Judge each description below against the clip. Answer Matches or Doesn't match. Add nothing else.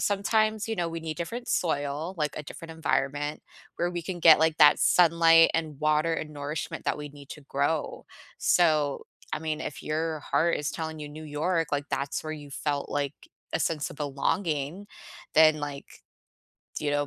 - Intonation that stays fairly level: Matches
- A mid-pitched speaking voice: Matches